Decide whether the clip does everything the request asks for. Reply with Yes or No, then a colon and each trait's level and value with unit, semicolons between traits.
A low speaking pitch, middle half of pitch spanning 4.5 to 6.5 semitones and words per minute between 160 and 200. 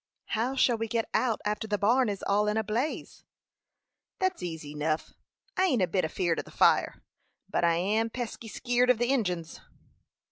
No: high, 215 Hz; average, 5.2 semitones; average, 185 wpm